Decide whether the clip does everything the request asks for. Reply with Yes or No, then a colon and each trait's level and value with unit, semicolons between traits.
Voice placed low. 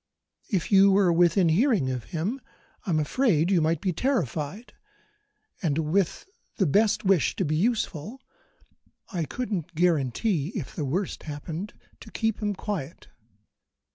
No: medium, 180 Hz